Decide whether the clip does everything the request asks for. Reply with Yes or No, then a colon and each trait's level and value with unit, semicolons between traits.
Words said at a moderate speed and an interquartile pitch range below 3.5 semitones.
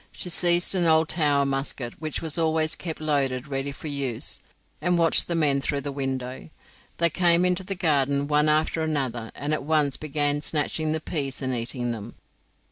Yes: average, 185 wpm; average, 2.8 semitones